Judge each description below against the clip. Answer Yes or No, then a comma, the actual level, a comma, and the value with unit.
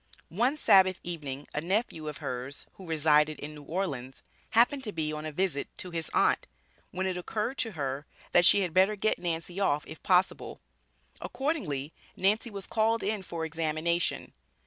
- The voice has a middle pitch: Yes, medium, 170 Hz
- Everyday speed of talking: Yes, average, 170 wpm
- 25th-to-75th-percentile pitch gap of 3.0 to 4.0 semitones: No, average, 4.6 semitones